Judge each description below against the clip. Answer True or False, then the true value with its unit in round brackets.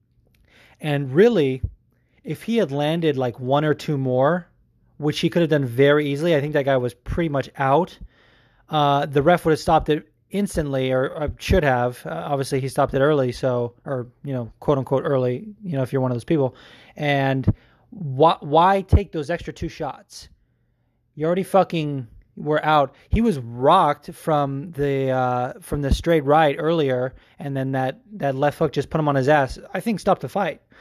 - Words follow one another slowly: False (195 wpm)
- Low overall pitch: False (145 Hz)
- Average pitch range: True (3.8 semitones)